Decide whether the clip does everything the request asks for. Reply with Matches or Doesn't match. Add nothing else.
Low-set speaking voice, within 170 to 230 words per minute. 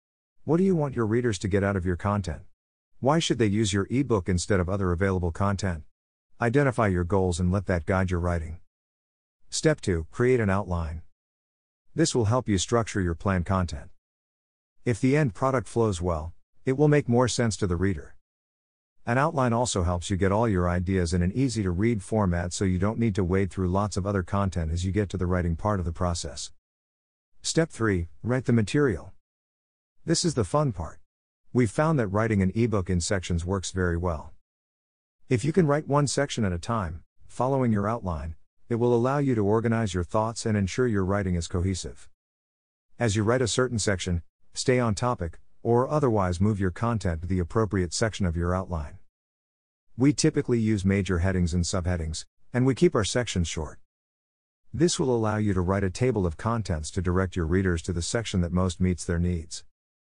Matches